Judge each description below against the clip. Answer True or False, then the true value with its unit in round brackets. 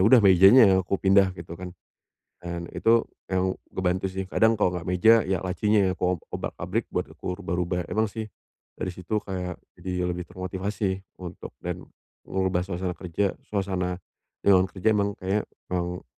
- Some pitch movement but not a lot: False (1.8 semitones)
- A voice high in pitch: False (95 Hz)